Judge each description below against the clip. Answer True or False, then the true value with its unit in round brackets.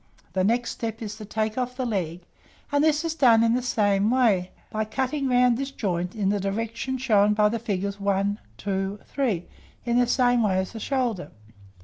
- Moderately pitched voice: False (220 Hz)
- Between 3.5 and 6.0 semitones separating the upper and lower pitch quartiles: True (3.8 semitones)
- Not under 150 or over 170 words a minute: False (200 wpm)